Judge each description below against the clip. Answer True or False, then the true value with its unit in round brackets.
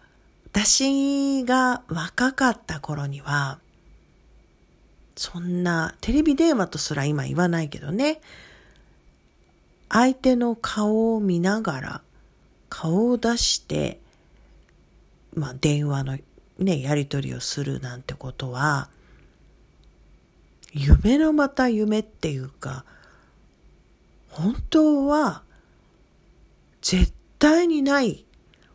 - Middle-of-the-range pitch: True (175 Hz)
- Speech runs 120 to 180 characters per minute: True (165 characters per minute)